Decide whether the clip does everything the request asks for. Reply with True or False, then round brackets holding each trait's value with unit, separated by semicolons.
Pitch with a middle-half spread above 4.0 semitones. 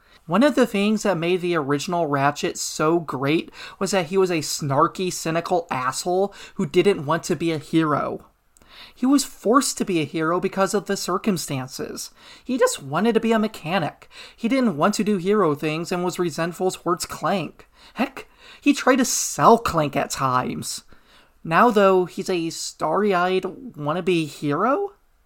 True (4.4 semitones)